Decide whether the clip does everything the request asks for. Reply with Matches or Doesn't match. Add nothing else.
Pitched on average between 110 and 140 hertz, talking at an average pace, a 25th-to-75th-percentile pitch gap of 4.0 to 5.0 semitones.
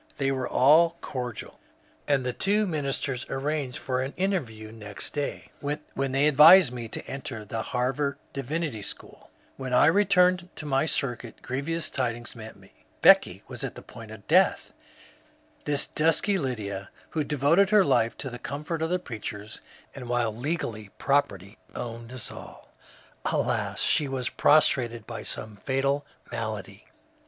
Matches